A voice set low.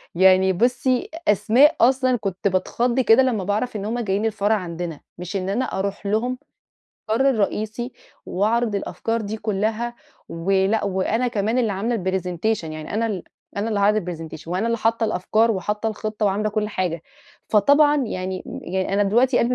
No: high, 210 Hz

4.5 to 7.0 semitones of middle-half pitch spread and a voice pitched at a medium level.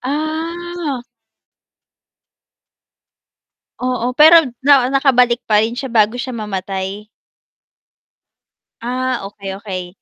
No: average, 4.8 semitones; very high, 250 Hz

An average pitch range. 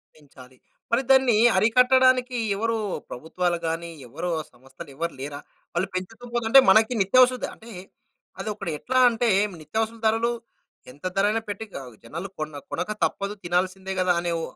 No: wide, 5.9 semitones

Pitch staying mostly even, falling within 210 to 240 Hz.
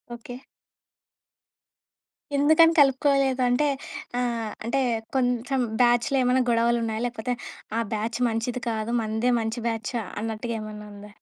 Yes: narrow, 2.2 semitones; high, 235 Hz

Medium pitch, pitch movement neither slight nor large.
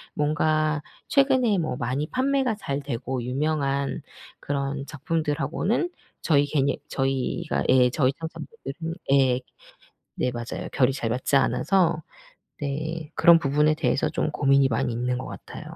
Yes: medium, 145 Hz; average, 3.3 semitones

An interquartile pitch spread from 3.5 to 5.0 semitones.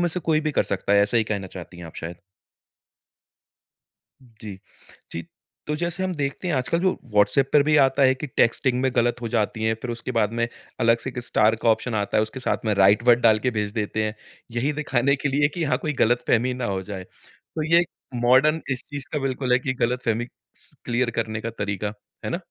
Yes: average, 4.2 semitones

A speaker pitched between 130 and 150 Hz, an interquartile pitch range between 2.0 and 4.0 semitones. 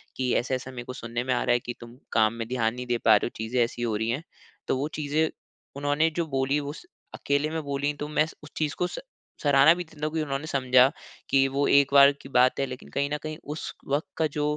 Yes: medium, 140 Hz; average, 3.0 semitones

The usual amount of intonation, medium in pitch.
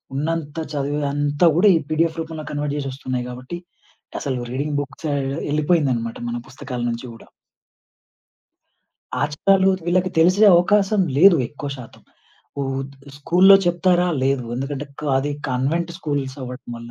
Yes: average, 4.1 semitones; medium, 145 Hz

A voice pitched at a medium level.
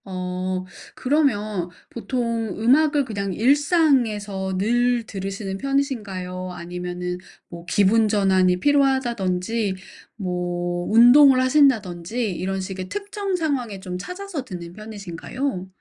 No: high, 210 Hz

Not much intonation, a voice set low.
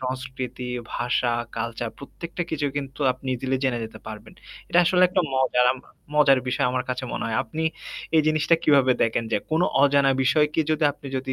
No: average, 3.1 semitones; low, 130 Hz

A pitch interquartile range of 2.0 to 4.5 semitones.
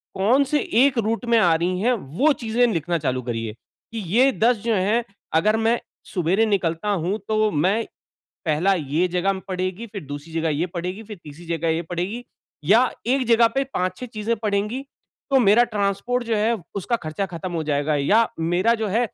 No: average, 5.3 semitones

